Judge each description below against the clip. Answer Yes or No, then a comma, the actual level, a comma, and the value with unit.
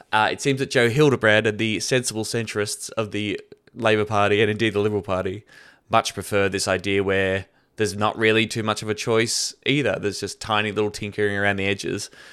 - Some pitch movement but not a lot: No, narrow, 1.7 semitones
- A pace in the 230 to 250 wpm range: No, average, 200 wpm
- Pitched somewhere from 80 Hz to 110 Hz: Yes, low, 105 Hz